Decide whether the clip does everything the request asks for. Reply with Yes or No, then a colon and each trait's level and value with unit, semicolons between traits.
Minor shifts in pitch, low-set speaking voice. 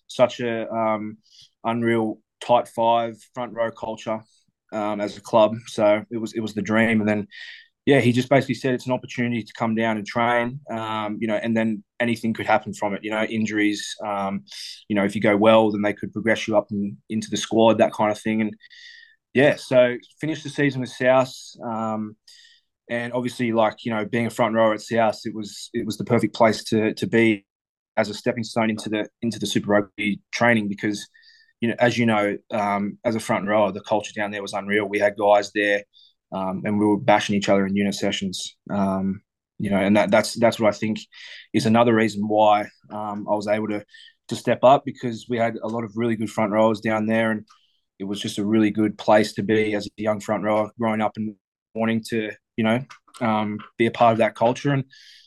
Yes: narrow, 2.0 semitones; low, 110 Hz